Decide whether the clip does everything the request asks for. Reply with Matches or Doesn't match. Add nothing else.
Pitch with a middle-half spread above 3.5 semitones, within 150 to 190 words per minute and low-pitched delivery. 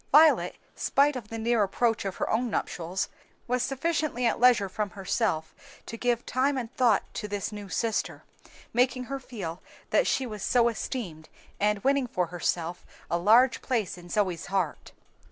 Doesn't match